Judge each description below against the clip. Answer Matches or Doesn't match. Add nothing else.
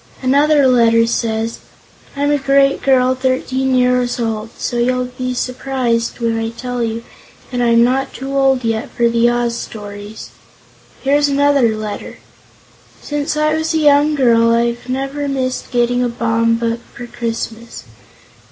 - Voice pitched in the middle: Doesn't match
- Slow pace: Doesn't match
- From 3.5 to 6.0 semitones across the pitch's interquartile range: Doesn't match